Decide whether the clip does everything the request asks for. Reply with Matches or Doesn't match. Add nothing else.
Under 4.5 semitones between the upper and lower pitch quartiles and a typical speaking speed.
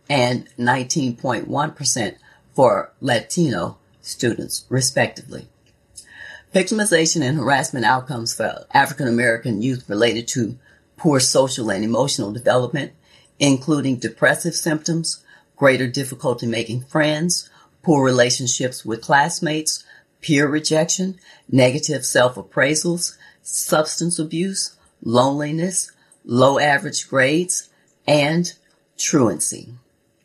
Doesn't match